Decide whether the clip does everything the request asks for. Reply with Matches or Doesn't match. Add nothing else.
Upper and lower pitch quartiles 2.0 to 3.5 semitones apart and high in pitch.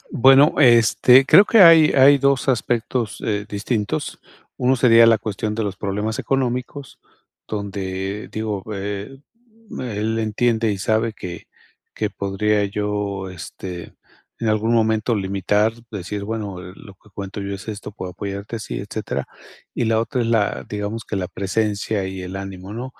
Doesn't match